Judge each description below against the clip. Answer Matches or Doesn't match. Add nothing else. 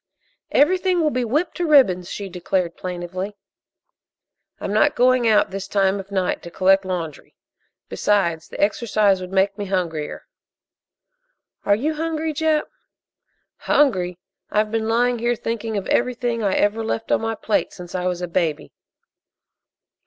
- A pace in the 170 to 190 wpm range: Doesn't match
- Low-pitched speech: Doesn't match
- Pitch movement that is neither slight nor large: Matches